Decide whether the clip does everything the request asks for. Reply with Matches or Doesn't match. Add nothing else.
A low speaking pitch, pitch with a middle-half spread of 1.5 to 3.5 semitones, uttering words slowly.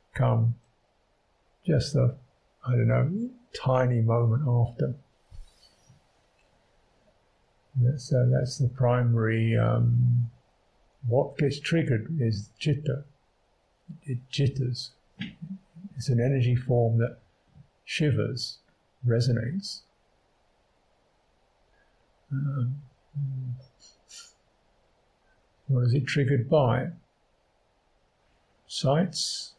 Matches